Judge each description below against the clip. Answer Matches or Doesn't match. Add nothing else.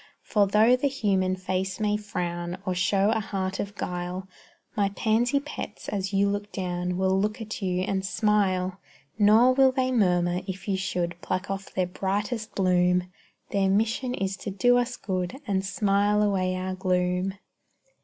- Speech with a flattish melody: Matches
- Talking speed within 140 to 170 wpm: Matches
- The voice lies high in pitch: Matches